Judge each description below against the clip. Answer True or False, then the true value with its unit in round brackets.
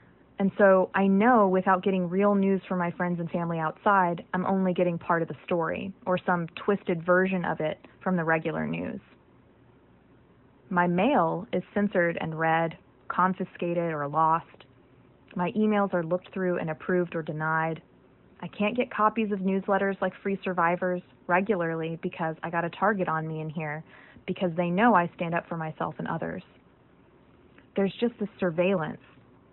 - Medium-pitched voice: True (180 Hz)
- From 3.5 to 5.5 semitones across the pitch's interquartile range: False (2.9 semitones)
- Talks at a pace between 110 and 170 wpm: True (165 wpm)